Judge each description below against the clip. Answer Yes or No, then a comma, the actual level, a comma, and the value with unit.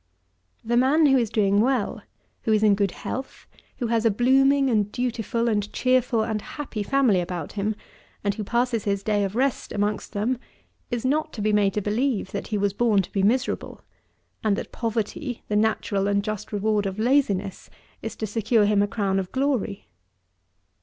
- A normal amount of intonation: Yes, average, 3.3 semitones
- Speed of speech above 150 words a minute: Yes, average, 190 wpm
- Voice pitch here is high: Yes, high, 215 Hz